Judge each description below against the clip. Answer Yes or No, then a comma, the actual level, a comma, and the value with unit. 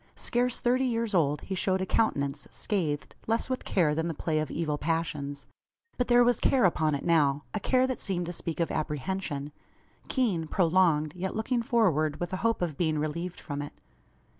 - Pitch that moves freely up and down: Yes, wide, 6.4 semitones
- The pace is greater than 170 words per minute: Yes, average, 190 wpm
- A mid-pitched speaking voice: Yes, medium, 170 Hz